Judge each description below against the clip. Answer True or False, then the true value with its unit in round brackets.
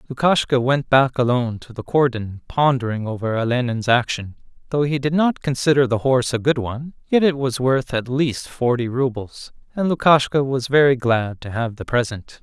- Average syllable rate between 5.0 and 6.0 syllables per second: True (5.1 syllables/s)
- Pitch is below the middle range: True (130 Hz)